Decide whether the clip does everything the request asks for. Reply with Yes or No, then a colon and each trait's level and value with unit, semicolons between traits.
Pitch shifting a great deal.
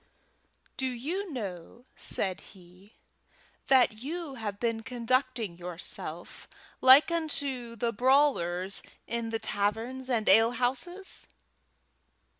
No: average, 4.1 semitones